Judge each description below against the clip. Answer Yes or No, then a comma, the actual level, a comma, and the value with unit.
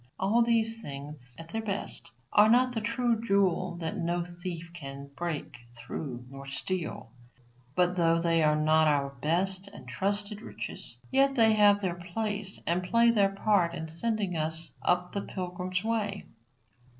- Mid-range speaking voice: Yes, medium, 180 Hz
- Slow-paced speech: No, average, 160 wpm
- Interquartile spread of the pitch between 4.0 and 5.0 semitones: Yes, average, 4.5 semitones